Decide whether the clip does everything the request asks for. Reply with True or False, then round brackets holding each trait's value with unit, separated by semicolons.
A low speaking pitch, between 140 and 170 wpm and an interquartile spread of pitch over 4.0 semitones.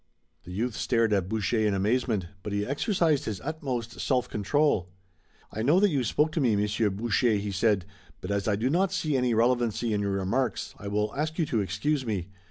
False (115 Hz; 205 wpm; 4.7 semitones)